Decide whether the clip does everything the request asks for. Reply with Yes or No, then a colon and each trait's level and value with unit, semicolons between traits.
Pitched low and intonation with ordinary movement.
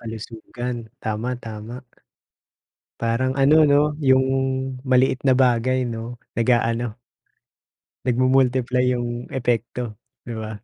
No: low, 120 Hz; narrow, 2.0 semitones